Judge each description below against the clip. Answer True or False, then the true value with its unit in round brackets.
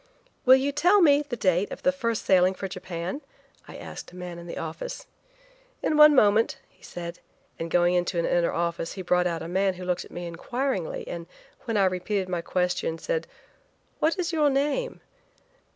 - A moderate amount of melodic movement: False (7.6 semitones)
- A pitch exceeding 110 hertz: True (185 Hz)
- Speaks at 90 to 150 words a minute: False (195 wpm)